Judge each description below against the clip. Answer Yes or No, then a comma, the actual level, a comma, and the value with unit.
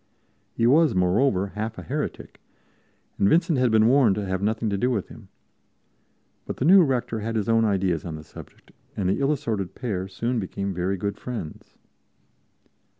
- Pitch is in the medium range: No, low, 110 Hz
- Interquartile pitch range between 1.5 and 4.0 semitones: No, average, 4.5 semitones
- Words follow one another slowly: No, average, 180 wpm